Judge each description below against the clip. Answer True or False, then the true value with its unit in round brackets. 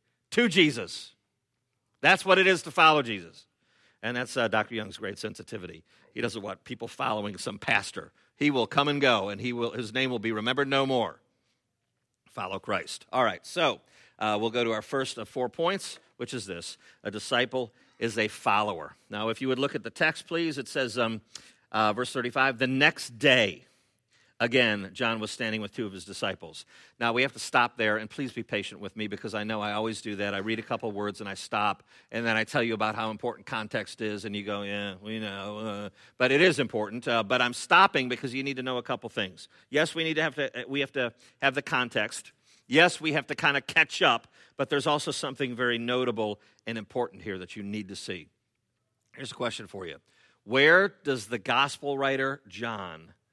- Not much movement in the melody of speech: False (4.1 semitones)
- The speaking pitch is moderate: False (120 Hz)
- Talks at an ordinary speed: False (215 wpm)